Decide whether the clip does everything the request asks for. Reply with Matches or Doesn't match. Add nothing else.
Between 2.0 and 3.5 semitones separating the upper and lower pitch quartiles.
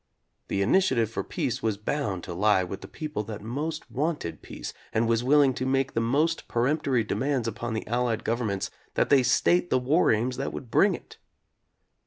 Doesn't match